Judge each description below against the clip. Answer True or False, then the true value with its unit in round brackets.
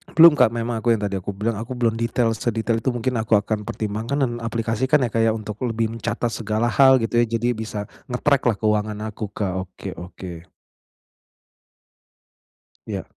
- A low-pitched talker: True (115 Hz)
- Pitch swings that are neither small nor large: False (2.0 semitones)